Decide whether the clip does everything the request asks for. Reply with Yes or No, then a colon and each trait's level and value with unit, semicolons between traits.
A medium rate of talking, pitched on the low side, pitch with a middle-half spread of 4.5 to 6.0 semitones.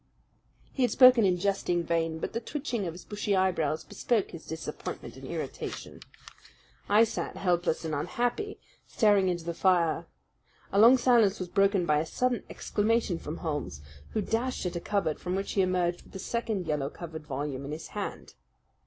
No: average, 180 wpm; medium, 185 Hz; average, 4.8 semitones